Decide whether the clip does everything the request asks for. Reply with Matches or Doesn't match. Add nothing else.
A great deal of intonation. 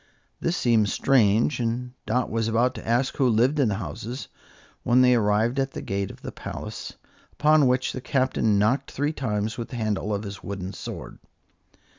Doesn't match